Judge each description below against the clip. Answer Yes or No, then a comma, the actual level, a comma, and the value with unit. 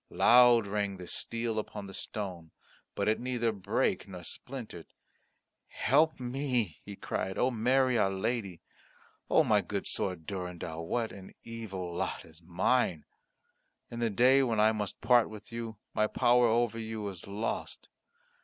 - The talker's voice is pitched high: No, low, 110 Hz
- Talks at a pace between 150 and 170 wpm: Yes, average, 155 wpm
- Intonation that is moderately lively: Yes, average, 4.0 semitones